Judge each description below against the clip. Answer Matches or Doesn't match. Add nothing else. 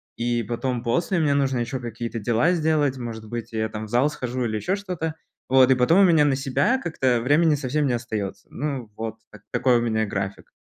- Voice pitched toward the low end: Matches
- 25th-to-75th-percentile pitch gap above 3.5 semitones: Matches